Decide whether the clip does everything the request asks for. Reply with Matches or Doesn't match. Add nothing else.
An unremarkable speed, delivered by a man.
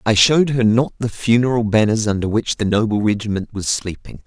Matches